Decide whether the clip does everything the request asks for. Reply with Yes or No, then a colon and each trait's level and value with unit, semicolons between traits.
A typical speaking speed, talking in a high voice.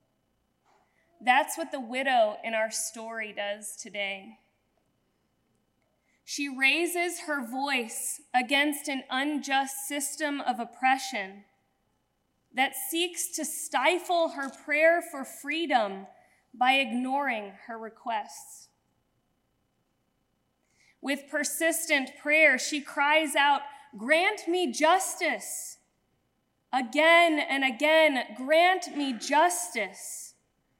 No: slow, 90 wpm; very high, 280 Hz